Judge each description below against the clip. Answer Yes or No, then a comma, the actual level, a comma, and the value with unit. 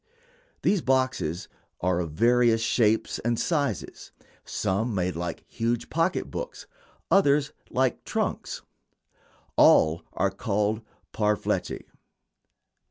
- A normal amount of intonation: No, wide, 5.8 semitones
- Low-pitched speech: Yes, low, 115 Hz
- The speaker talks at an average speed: No, slow, 100 wpm